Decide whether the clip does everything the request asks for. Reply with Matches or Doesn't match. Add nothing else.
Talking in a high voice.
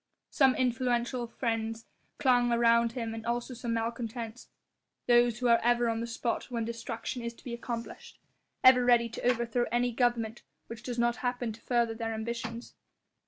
Matches